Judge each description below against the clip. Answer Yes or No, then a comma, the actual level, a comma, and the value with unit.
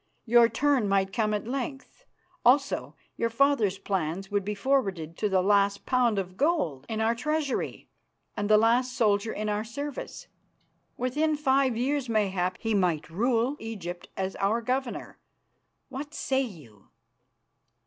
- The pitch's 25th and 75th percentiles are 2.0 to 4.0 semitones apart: No, average, 5.0 semitones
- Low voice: No, high, 225 Hz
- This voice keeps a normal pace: Yes, average, 145 wpm